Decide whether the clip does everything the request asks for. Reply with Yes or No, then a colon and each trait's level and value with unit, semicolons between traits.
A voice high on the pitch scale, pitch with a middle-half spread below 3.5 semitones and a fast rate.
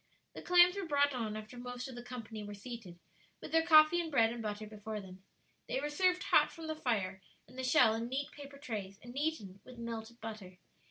No: high, 240 Hz; average, 5.1 semitones; fast, 225 wpm